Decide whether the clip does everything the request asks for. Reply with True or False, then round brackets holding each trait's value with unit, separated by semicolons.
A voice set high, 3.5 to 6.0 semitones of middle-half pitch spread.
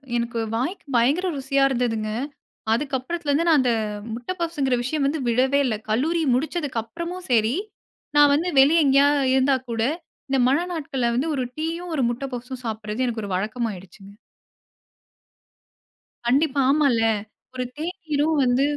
True (270 Hz; 4.3 semitones)